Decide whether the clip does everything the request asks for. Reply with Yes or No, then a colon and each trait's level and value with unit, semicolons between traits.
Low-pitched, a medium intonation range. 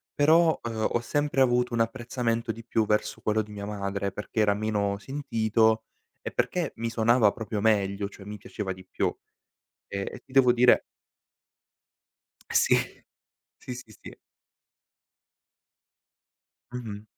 Yes: low, 110 Hz; average, 3.0 semitones